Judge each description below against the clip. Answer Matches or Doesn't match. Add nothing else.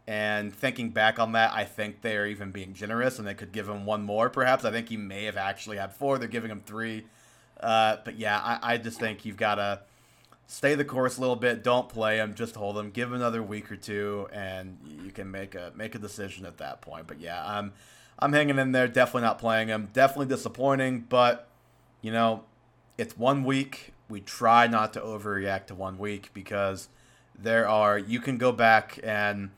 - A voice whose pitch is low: Matches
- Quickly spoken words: Matches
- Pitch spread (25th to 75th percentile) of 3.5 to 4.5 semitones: Doesn't match